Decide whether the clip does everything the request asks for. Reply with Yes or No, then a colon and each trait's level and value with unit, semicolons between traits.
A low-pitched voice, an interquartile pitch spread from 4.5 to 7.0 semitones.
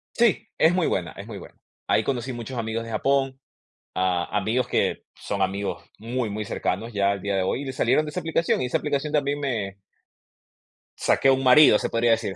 Yes: low, 115 Hz; average, 5.3 semitones